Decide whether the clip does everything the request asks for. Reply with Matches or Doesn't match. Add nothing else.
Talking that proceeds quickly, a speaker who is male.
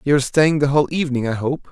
Matches